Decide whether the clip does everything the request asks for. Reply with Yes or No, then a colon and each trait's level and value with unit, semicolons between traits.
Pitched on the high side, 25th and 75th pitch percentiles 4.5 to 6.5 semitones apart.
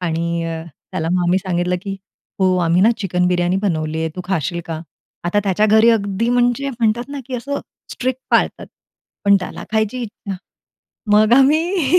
Yes: high, 200 Hz; average, 5.1 semitones